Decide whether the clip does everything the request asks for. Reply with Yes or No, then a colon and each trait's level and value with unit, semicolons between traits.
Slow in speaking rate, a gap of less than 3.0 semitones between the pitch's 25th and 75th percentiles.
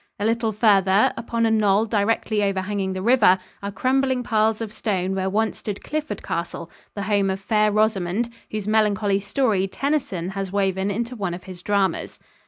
No: average, 175 wpm; narrow, 2.5 semitones